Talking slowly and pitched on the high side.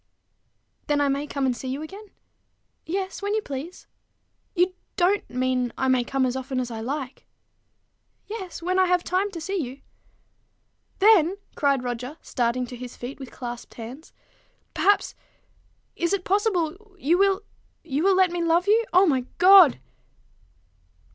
No: average, 160 wpm; very high, 320 Hz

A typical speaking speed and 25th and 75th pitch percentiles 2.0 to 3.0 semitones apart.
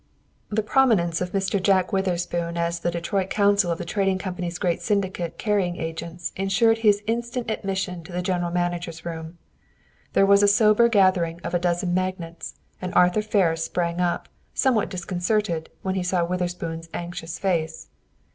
Yes: average, 160 wpm; narrow, 2.6 semitones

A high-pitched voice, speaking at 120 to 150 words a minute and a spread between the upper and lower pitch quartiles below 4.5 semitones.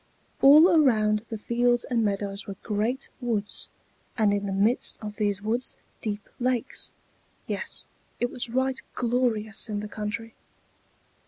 Yes: high, 220 Hz; average, 140 wpm; average, 2.7 semitones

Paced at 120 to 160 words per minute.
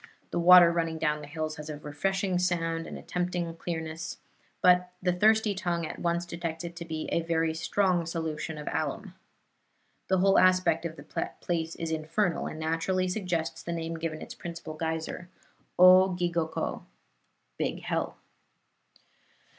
Yes: average, 155 wpm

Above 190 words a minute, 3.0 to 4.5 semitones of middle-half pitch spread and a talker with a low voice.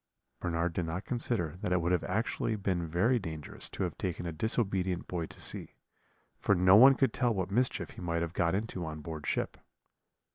Yes: fast, 205 wpm; average, 4.1 semitones; very low, 90 Hz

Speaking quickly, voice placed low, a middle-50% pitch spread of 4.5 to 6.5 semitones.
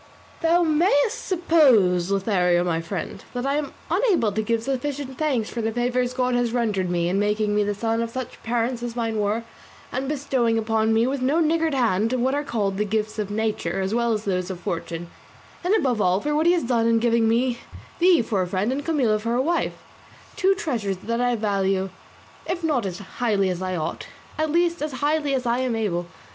No: fast, 210 wpm; high, 230 Hz; average, 5.0 semitones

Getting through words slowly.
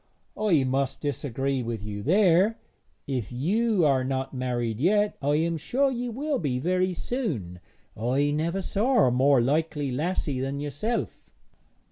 No: average, 145 wpm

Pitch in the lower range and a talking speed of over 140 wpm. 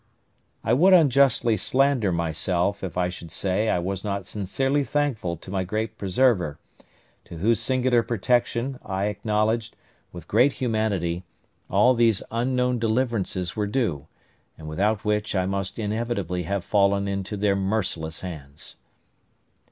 No: low, 105 Hz; slow, 135 wpm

